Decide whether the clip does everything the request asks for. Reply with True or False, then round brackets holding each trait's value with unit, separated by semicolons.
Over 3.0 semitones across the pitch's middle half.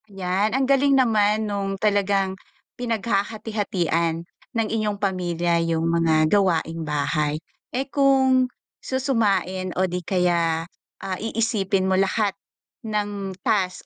True (4.0 semitones)